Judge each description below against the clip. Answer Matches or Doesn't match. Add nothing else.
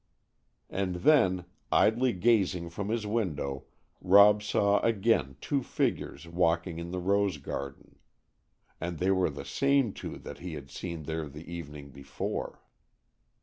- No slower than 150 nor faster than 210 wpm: Doesn't match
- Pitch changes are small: Doesn't match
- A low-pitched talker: Matches